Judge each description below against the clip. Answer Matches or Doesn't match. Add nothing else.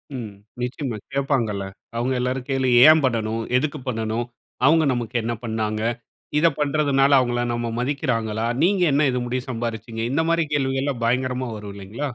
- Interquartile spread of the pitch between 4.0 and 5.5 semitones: Doesn't match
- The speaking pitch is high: Doesn't match